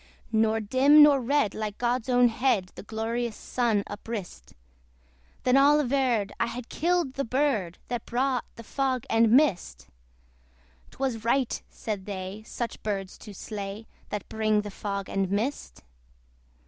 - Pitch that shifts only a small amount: No, average, 3.9 semitones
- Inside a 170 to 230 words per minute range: No, average, 145 wpm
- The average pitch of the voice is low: No, high, 230 Hz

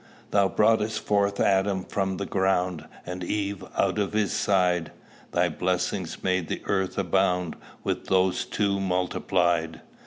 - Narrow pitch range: Yes, narrow, 1.8 semitones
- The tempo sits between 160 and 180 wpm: No, slow, 135 wpm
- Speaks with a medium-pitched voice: No, very low, 95 Hz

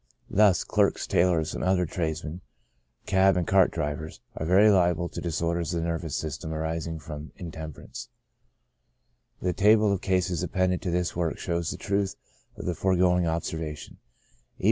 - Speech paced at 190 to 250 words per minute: No, average, 165 wpm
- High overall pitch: No, very low, 85 Hz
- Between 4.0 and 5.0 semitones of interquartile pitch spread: No, narrow, 2.5 semitones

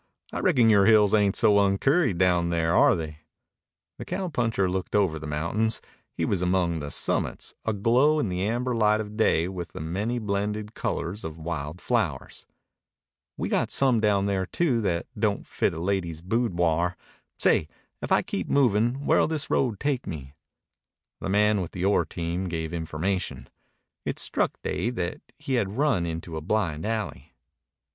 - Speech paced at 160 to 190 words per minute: Yes, average, 165 wpm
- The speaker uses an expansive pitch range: No, average, 4.7 semitones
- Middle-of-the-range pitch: No, low, 100 Hz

